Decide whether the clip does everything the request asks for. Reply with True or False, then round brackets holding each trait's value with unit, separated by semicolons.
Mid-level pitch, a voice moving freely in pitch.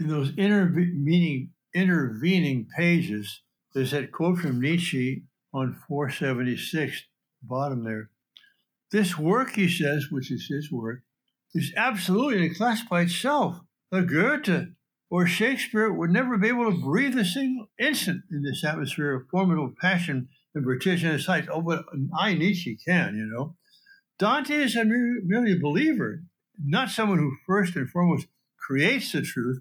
True (170 Hz; 5.9 semitones)